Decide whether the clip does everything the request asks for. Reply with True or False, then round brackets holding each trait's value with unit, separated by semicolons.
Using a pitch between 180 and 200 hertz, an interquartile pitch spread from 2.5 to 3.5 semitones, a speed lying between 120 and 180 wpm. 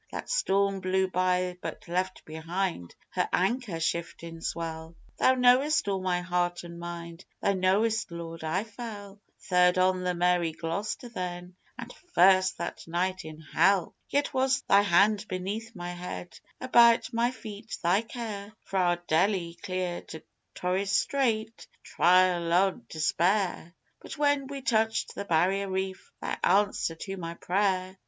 True (185 Hz; 3.2 semitones; 145 wpm)